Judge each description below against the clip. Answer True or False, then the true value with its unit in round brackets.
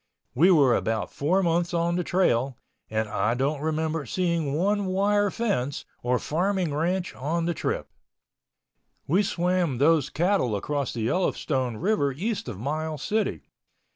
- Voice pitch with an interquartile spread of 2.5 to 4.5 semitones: False (5.1 semitones)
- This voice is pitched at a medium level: True (160 Hz)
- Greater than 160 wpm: False (150 wpm)